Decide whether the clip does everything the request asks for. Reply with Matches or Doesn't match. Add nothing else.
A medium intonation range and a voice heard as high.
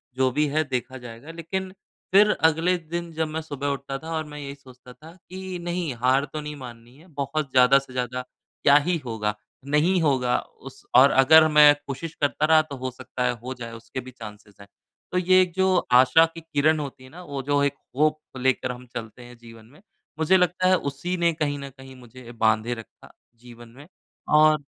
Doesn't match